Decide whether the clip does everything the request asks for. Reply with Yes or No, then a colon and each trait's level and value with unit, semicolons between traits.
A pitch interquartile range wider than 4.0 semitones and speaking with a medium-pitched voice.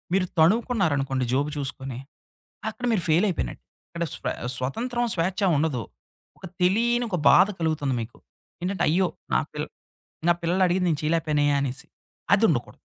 Yes: average, 5.2 semitones; medium, 165 Hz